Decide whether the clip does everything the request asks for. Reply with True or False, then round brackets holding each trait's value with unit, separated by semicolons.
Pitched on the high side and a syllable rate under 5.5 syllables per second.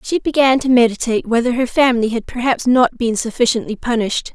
False (240 Hz; 6.1 syllables/s)